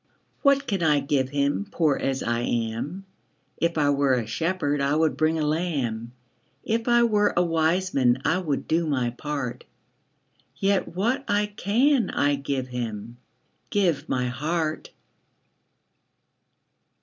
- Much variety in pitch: Yes, wide, 6.0 semitones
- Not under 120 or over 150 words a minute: Yes, average, 140 wpm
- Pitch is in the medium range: Yes, medium, 150 Hz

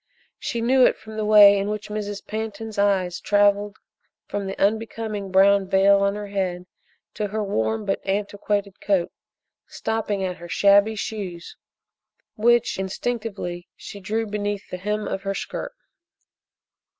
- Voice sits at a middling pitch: No, high, 205 Hz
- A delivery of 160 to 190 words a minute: No, average, 145 wpm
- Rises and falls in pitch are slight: Yes, narrow, 1.7 semitones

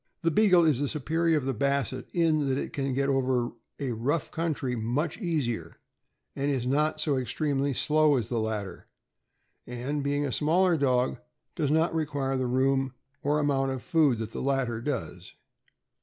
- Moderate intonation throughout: Yes, average, 3.2 semitones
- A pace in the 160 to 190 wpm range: Yes, average, 170 wpm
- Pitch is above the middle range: No, medium, 140 Hz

